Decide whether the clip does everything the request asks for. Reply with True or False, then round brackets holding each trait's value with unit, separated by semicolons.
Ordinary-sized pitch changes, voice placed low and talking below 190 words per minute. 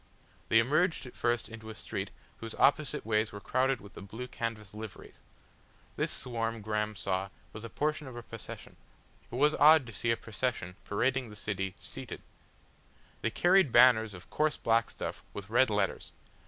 True (3.4 semitones; 115 Hz; 175 wpm)